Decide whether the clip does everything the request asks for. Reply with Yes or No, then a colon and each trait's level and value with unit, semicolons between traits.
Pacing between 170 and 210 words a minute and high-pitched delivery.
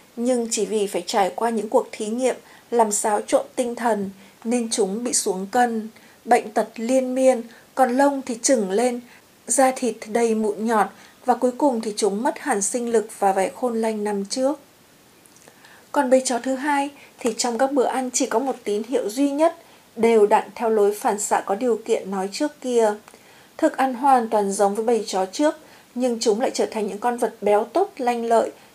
Yes: average, 205 wpm; high, 235 Hz